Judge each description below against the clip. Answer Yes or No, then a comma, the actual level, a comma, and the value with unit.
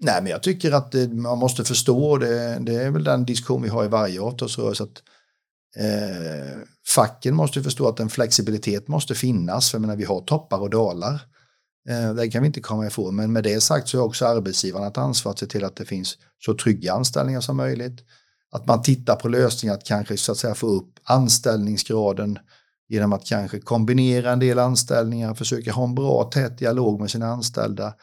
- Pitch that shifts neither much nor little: Yes, average, 3.3 semitones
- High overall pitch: No, low, 115 Hz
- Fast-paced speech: Yes, fast, 200 wpm